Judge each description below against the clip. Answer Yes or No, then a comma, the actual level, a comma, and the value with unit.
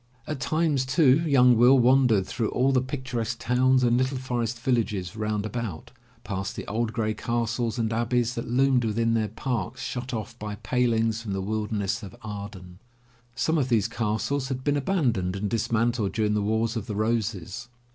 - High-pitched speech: No, low, 115 Hz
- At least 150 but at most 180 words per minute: Yes, average, 175 wpm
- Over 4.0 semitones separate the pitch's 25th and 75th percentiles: No, average, 3.0 semitones